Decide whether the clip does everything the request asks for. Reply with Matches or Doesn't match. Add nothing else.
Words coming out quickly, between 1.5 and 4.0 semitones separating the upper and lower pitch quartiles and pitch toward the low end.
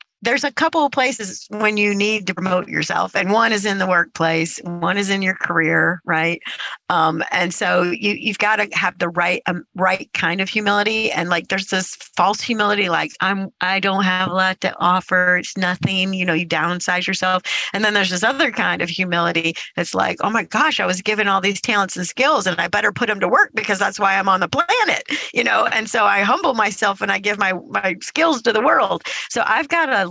Doesn't match